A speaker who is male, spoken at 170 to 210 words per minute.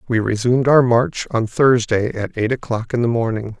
Yes: male; average, 200 wpm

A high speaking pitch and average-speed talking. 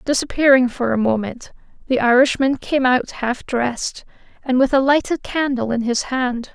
Yes: very high, 255 Hz; average, 165 wpm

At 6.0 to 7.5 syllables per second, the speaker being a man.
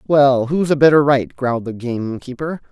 No: 5.1 syllables/s; male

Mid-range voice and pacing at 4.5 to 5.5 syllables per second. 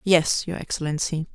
Yes: medium, 165 Hz; 5.0 syllables/s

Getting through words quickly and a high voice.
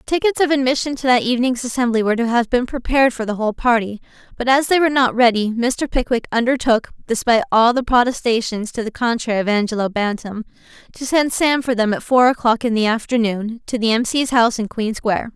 Yes: fast, 210 wpm; high, 240 Hz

